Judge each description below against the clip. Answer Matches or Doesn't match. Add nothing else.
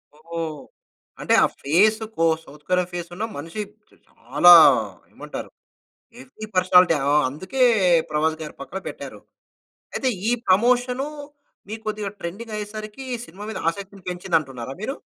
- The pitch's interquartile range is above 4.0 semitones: Matches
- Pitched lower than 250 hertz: Matches